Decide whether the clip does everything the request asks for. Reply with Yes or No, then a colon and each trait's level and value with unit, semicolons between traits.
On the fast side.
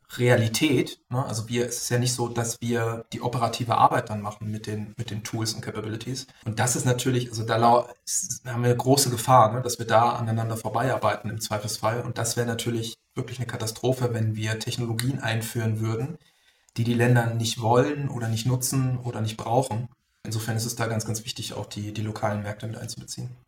Yes: fast, 210 wpm